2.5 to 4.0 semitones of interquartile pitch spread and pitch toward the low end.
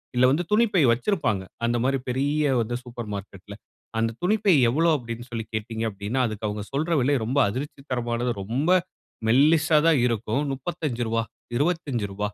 No: average, 5.0 semitones; low, 125 Hz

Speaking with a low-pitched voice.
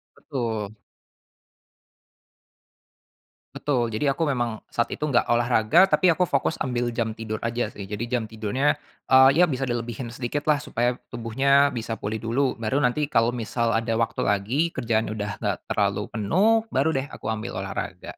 Yes: low, 120 Hz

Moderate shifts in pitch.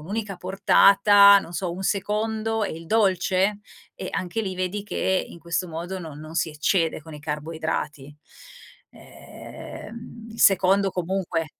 Yes: average, 3.5 semitones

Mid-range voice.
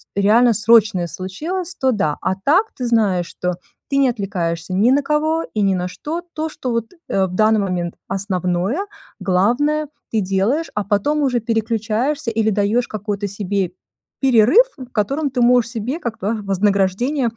No: high, 220 Hz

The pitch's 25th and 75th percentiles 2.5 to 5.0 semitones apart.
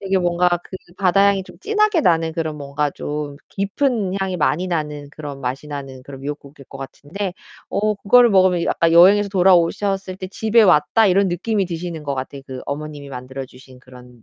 No: wide, 5.5 semitones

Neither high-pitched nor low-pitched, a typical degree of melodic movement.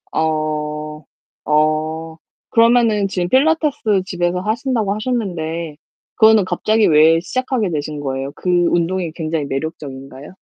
No: medium, 170 Hz; wide, 5.8 semitones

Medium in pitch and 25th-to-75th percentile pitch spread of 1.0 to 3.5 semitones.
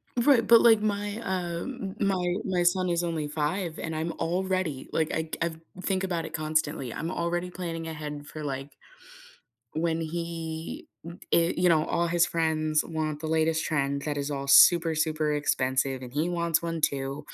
Yes: medium, 165 Hz; narrow, 2.4 semitones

